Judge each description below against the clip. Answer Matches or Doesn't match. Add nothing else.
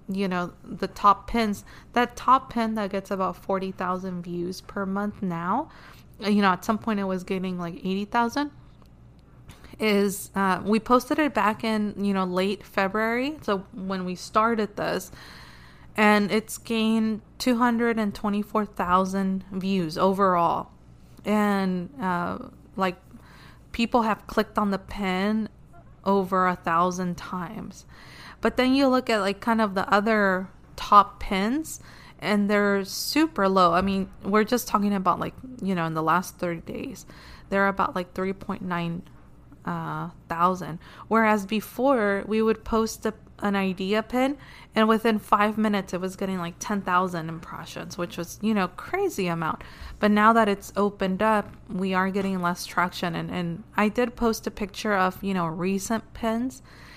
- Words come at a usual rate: Matches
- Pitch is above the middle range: Matches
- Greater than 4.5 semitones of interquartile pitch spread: Doesn't match